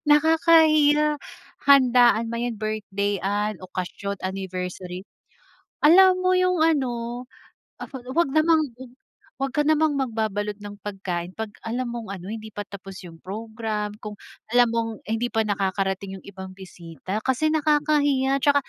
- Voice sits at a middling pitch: No, high, 225 Hz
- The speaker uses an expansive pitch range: Yes, wide, 6.5 semitones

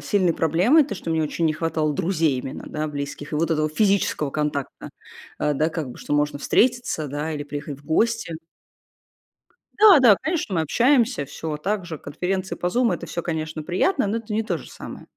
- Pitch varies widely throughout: Yes, wide, 5.8 semitones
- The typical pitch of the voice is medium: Yes, medium, 165 Hz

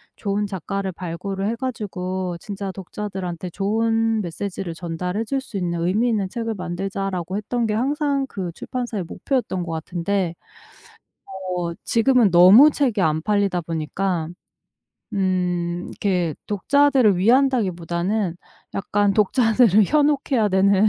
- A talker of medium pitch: No, high, 195 Hz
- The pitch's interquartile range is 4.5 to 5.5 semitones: No, average, 4.1 semitones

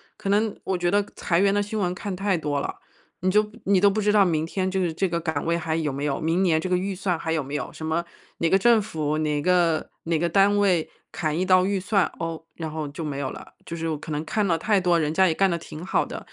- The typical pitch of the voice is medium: Yes, medium, 175 Hz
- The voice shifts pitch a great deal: No, average, 3.4 semitones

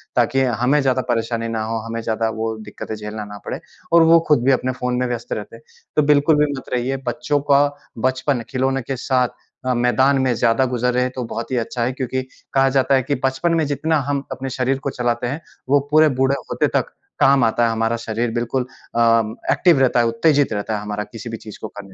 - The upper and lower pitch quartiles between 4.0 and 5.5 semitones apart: No, average, 2.8 semitones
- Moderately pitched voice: No, low, 125 Hz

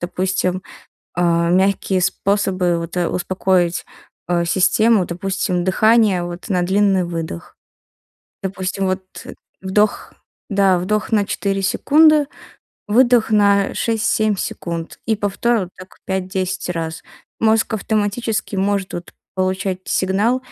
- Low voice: No, high, 190 Hz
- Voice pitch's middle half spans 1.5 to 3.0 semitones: Yes, narrow, 2.5 semitones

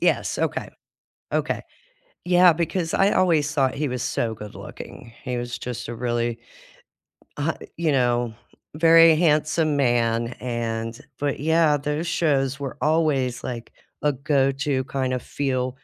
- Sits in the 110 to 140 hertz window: Yes, low, 135 Hz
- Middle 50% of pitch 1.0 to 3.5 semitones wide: No, average, 4.1 semitones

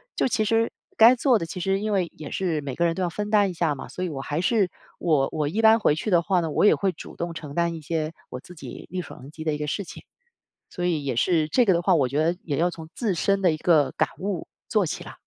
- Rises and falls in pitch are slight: No, average, 4.2 semitones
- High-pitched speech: No, medium, 170 Hz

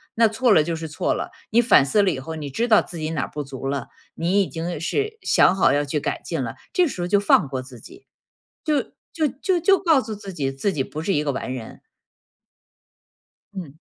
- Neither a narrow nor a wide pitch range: No, wide, 8.2 semitones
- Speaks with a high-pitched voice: No, medium, 175 Hz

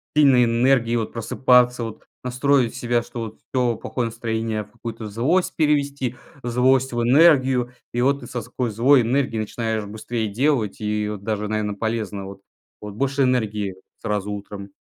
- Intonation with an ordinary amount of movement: Yes, average, 3.1 semitones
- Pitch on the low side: Yes, low, 120 Hz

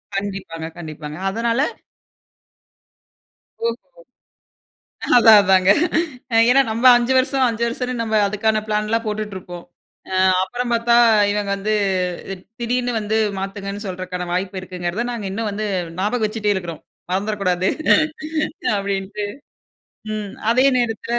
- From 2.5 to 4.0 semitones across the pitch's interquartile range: Yes, average, 3.4 semitones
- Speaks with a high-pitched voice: Yes, high, 210 Hz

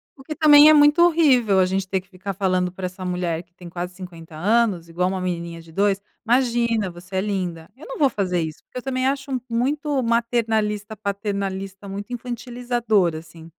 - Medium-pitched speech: No, high, 200 Hz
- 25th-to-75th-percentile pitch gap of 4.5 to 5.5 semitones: Yes, average, 5.0 semitones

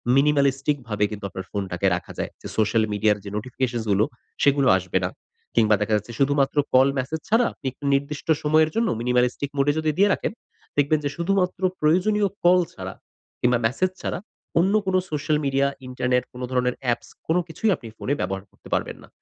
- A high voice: No, low, 135 Hz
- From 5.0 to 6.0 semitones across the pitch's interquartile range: Yes, average, 5.3 semitones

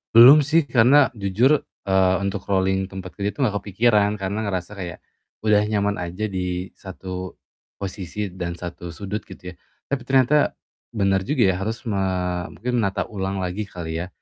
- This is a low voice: Yes, low, 100 Hz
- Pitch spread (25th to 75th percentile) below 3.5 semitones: Yes, average, 2.8 semitones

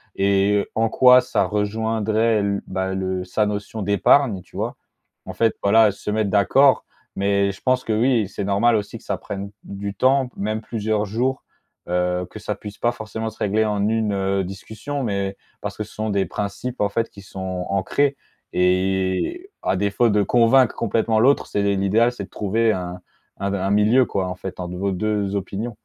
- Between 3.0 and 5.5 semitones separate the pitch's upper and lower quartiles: No, narrow, 2.5 semitones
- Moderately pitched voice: No, low, 105 Hz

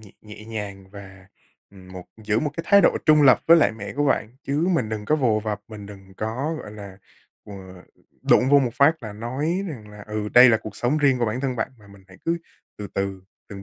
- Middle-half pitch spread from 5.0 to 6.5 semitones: Yes, average, 5.3 semitones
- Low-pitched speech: Yes, low, 110 Hz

